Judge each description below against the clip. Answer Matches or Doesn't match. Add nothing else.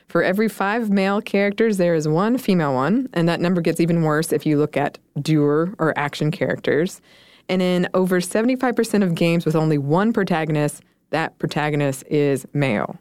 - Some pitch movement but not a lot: Matches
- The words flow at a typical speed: Matches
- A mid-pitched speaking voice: Matches